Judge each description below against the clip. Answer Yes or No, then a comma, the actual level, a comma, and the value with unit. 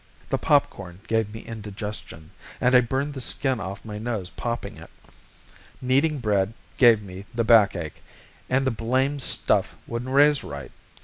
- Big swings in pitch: No, average, 4.3 semitones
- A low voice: Yes, low, 115 Hz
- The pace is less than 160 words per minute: Yes, average, 150 wpm